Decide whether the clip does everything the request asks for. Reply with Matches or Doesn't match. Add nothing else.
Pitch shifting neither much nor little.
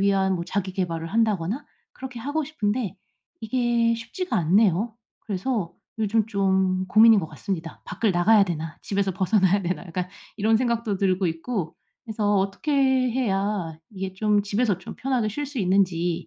Matches